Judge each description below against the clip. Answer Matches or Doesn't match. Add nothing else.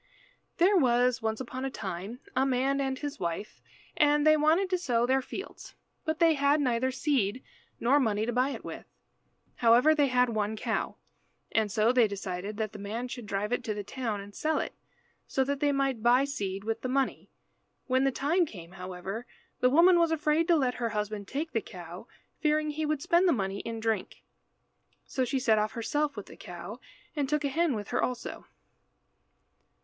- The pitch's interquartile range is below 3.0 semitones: Doesn't match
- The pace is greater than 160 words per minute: Matches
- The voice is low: Doesn't match